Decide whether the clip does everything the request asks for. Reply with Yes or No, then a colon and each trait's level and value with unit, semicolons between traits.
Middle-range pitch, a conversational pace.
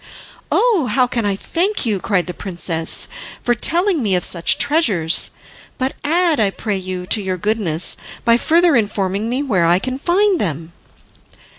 No: high, 215 Hz; average, 165 wpm